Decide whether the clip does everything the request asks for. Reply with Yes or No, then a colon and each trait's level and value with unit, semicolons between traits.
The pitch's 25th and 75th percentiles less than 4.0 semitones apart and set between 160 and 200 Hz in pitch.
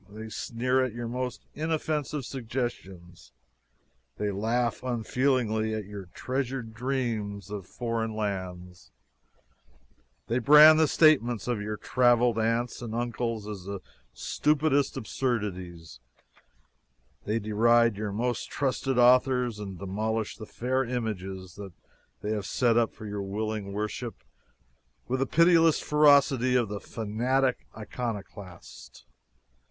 No: average, 3.6 semitones; low, 115 Hz